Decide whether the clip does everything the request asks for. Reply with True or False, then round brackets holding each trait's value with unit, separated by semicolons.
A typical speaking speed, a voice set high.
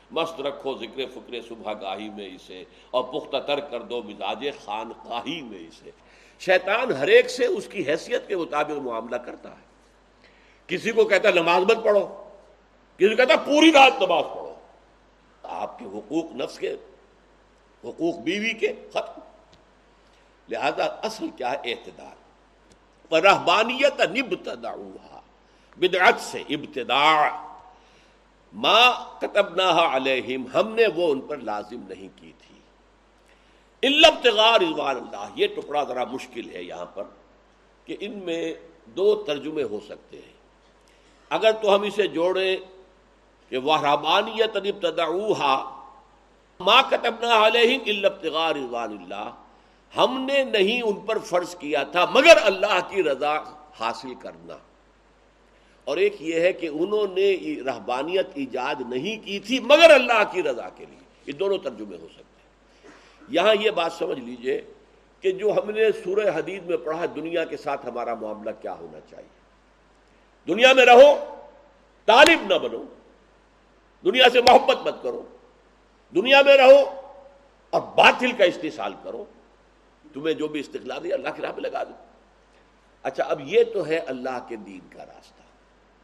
True (145 wpm; 210 Hz)